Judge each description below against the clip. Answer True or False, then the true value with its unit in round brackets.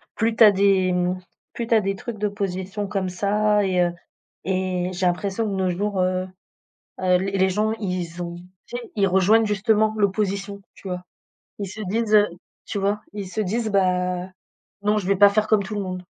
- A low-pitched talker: False (195 Hz)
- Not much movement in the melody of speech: True (2.3 semitones)